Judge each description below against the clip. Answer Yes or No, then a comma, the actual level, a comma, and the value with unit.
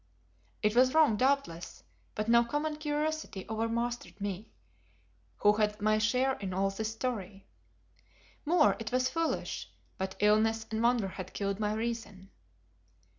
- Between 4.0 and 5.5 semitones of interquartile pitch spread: No, average, 3.6 semitones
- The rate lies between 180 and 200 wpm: No, average, 140 wpm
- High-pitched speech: Yes, high, 220 Hz